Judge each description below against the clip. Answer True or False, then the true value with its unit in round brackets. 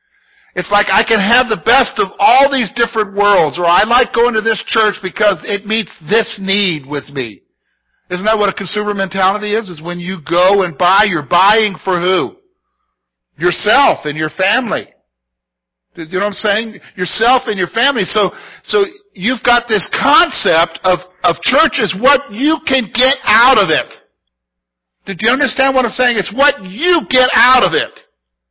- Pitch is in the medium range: False (210 Hz)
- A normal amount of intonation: False (5.9 semitones)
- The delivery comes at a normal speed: True (180 wpm)